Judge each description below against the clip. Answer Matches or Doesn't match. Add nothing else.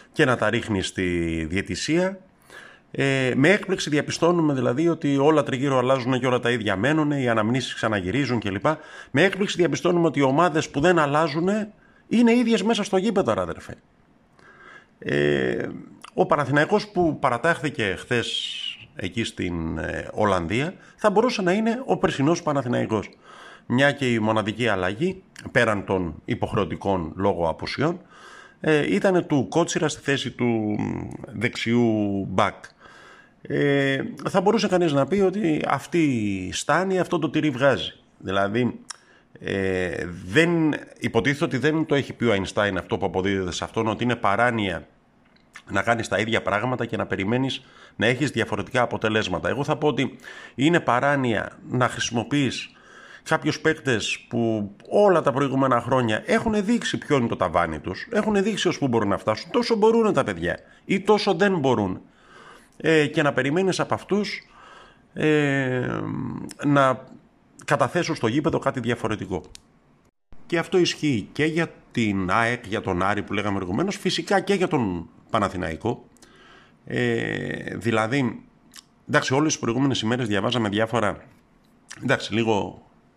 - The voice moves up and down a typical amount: Doesn't match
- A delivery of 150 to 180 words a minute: Doesn't match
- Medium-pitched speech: Doesn't match